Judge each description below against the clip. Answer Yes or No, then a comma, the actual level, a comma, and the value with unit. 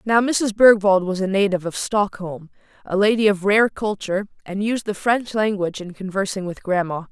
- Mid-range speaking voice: No, high, 200 Hz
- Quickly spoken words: No, average, 185 wpm